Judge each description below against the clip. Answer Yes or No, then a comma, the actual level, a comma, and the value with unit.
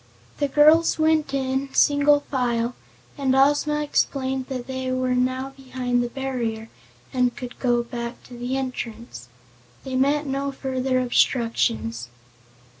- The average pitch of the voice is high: Yes, very high, 260 Hz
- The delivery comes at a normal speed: No, slow, 130 wpm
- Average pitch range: No, narrow, 2.0 semitones